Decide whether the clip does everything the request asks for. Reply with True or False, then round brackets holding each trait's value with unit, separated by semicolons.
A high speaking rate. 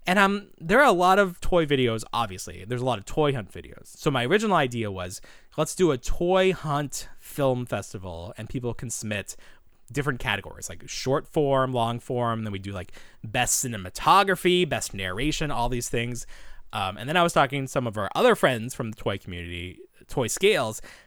False (195 wpm)